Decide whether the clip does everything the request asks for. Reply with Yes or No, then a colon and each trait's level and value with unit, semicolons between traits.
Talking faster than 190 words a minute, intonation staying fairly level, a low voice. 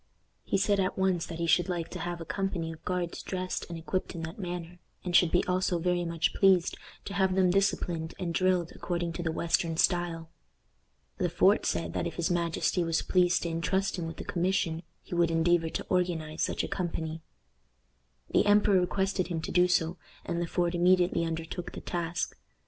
No: average, 200 wpm; narrow, 1.7 semitones; medium, 175 Hz